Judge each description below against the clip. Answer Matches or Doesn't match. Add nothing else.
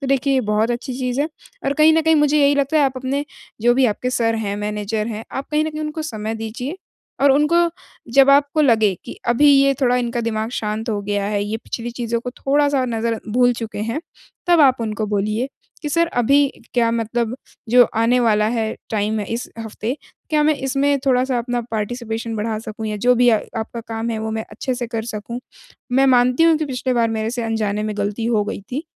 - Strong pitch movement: Doesn't match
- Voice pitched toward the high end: Matches